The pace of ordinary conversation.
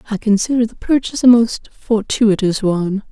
Yes: average, 155 wpm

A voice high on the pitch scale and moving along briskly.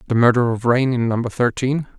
No: low, 120 Hz; fast, 210 wpm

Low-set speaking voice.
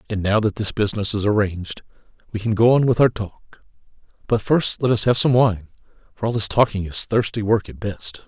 Yes: low, 105 Hz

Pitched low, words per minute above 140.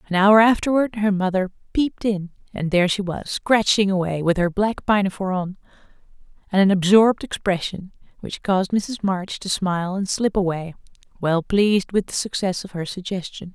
No: high, 195 Hz; average, 175 wpm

